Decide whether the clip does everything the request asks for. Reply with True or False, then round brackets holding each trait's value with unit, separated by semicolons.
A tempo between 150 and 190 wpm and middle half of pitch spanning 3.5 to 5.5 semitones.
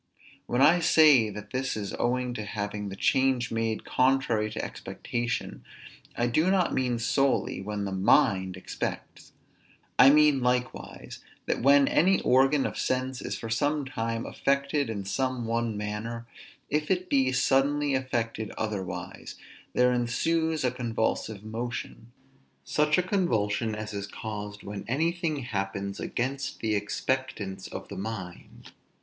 False (140 wpm; 4.3 semitones)